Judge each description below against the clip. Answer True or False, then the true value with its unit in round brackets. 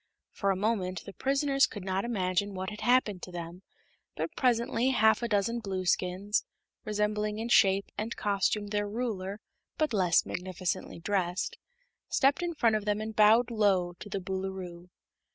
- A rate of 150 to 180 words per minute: True (160 wpm)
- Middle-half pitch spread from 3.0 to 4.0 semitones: True (3.3 semitones)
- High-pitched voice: True (205 Hz)